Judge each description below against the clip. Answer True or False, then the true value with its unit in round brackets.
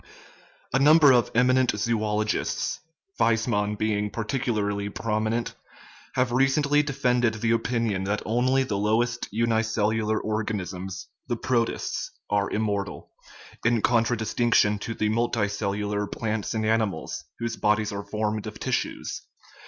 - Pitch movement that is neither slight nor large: False (2.2 semitones)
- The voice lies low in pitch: True (110 Hz)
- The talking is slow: True (115 wpm)